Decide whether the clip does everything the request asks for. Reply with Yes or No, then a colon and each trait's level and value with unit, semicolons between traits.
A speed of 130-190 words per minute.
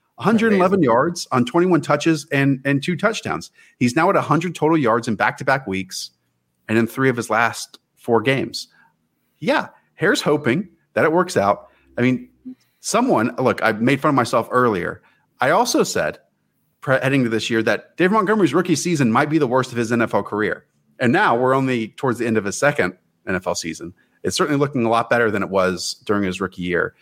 No: average, 200 wpm